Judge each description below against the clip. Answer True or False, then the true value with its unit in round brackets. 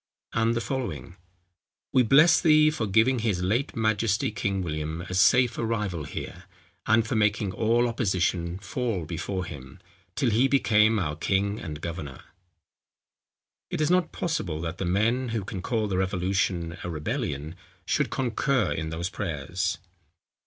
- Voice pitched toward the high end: False (100 Hz)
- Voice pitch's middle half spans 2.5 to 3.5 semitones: False (5.0 semitones)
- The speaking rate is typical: True (150 wpm)